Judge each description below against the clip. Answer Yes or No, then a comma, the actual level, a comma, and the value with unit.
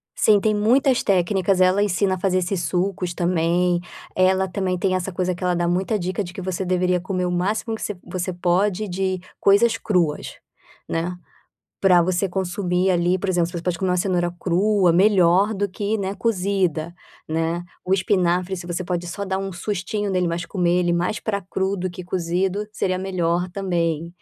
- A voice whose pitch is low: No, medium, 185 Hz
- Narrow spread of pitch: Yes, narrow, 1.8 semitones